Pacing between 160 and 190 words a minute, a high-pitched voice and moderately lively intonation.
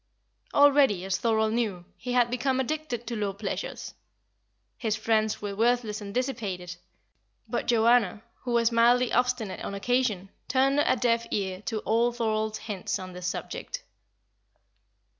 No: average, 140 wpm; high, 230 Hz; average, 3.2 semitones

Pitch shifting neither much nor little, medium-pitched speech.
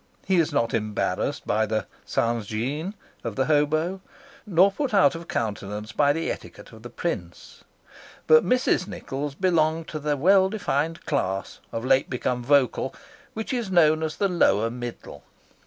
No: wide, 7.3 semitones; medium, 150 Hz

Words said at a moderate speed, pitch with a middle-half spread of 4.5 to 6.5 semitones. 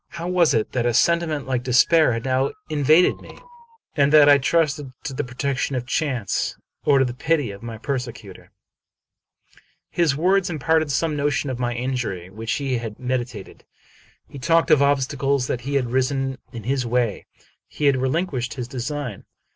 No: average, 170 wpm; average, 3.2 semitones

